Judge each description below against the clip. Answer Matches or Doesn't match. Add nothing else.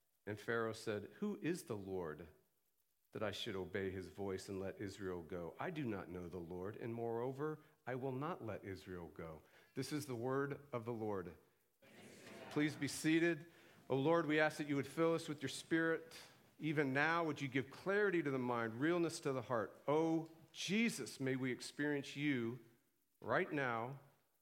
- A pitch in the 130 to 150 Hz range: Matches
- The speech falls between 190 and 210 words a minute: Doesn't match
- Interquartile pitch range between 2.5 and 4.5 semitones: Doesn't match